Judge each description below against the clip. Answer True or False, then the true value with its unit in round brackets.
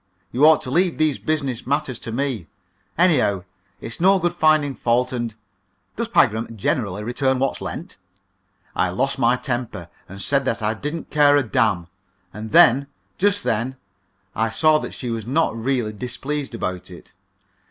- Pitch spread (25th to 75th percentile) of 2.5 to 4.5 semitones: False (4.9 semitones)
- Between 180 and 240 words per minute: False (165 wpm)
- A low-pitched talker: True (125 Hz)